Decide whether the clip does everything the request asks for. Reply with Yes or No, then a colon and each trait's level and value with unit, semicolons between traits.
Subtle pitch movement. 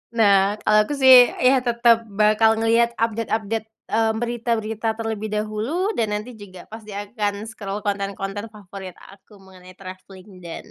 Yes: narrow, 2.3 semitones